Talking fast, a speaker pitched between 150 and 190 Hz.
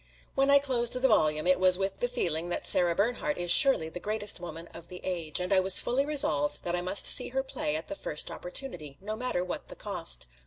Yes: fast, 235 wpm; medium, 185 Hz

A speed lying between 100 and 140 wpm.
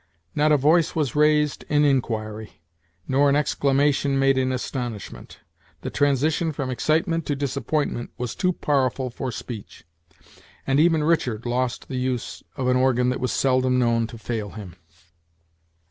No: average, 150 wpm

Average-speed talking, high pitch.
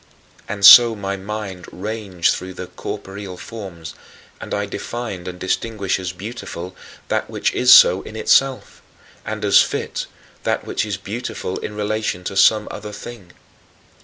No: average, 155 wpm; low, 100 Hz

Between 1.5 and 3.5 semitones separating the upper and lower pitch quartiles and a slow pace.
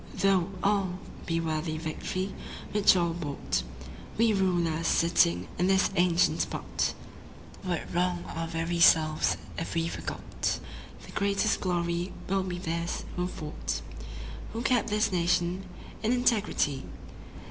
Yes: average, 2.8 semitones; slow, 125 wpm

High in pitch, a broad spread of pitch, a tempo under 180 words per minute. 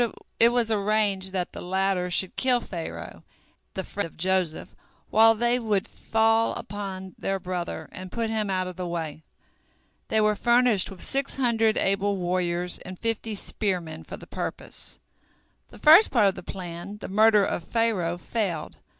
No: high, 195 Hz; average, 3.6 semitones; average, 165 wpm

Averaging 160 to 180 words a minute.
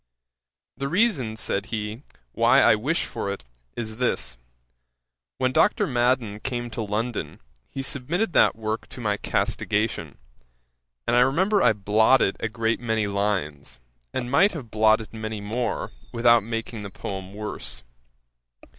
No: average, 140 wpm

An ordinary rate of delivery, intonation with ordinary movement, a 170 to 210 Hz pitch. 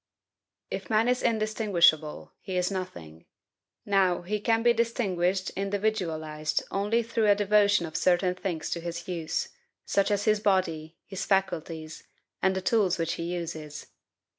Yes: average, 145 wpm; average, 3.7 semitones; high, 190 Hz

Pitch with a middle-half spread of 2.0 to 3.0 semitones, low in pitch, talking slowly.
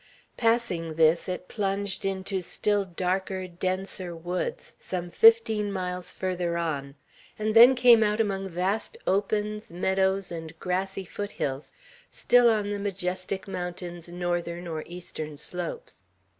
No: average, 2.7 semitones; medium, 185 Hz; slow, 130 wpm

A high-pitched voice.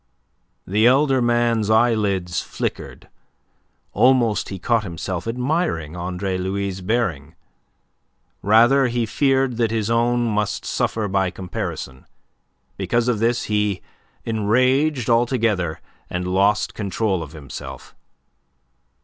No: low, 110 Hz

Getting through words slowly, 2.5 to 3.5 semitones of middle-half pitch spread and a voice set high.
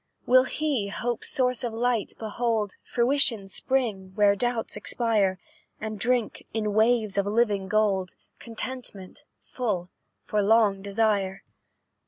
Yes: slow, 120 wpm; average, 3.2 semitones; high, 220 Hz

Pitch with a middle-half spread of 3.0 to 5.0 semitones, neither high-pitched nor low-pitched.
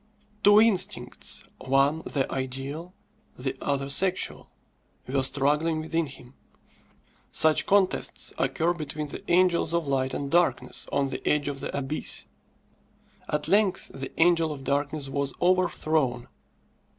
Yes: average, 3.8 semitones; medium, 150 Hz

